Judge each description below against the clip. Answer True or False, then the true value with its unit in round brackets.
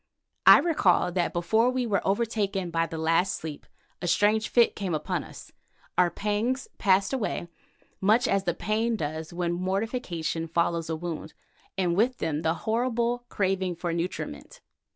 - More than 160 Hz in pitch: True (190 Hz)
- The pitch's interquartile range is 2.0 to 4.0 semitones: False (4.7 semitones)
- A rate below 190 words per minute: True (155 wpm)